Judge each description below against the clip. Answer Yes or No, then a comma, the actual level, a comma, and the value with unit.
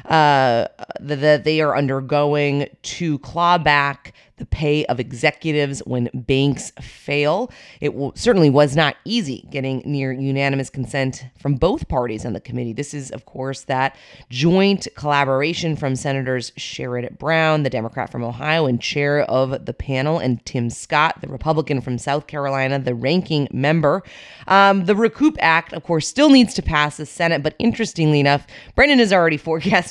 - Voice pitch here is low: No, medium, 145 Hz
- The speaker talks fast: No, average, 165 wpm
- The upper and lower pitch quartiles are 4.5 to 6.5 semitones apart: No, average, 3.3 semitones